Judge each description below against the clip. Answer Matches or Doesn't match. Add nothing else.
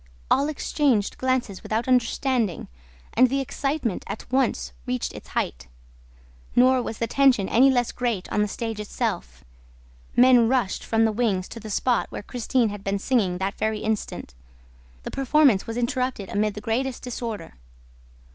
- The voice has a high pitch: Matches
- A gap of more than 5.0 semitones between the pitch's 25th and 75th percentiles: Doesn't match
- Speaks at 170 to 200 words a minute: Doesn't match